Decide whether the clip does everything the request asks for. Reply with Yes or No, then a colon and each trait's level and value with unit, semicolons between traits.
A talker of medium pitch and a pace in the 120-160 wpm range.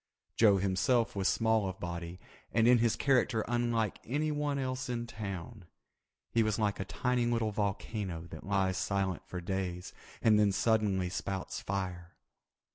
No: low, 105 Hz; average, 150 wpm